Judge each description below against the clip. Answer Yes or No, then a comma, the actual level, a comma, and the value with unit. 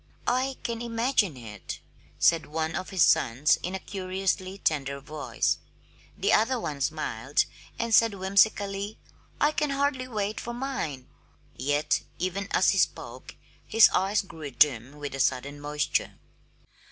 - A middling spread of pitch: No, wide, 7.5 semitones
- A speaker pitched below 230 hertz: Yes, medium, 185 Hz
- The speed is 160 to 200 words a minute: No, average, 140 wpm